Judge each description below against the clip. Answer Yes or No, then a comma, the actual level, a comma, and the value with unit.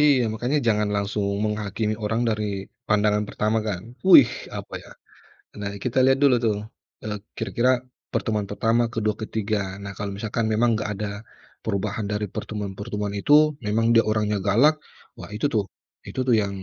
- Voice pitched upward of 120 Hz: No, low, 105 Hz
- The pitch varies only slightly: Yes, narrow, 1.7 semitones